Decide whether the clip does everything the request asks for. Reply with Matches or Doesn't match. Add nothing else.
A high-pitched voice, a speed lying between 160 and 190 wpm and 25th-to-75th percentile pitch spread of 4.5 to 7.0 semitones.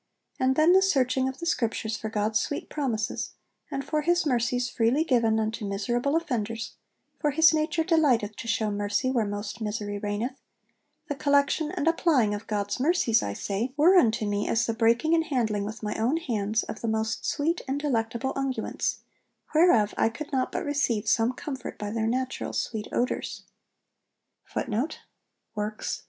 Matches